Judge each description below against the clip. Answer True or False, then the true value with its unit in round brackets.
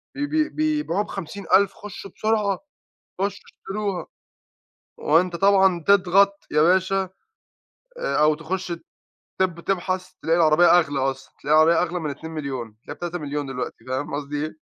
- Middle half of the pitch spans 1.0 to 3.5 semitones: False (4.2 semitones)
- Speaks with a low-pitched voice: False (175 Hz)